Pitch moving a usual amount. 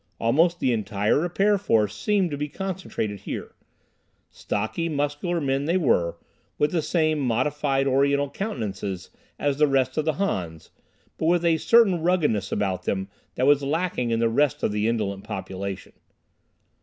No: wide, 7.4 semitones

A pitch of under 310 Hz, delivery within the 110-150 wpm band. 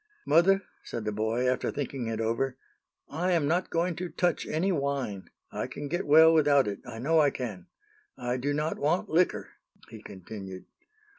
No: medium, 140 Hz; average, 175 wpm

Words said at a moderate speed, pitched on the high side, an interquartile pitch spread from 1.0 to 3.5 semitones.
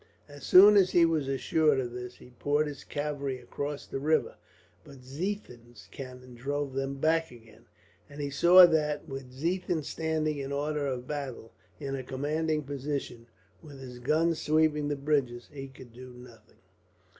No: average, 165 wpm; medium, 140 Hz; average, 3.1 semitones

